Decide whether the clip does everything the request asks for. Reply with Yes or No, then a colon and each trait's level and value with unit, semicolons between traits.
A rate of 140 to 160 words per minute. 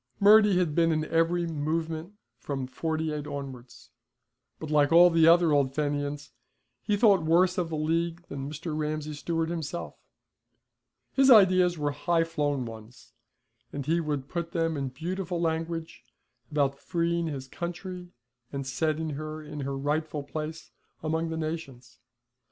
Yes: average, 150 wpm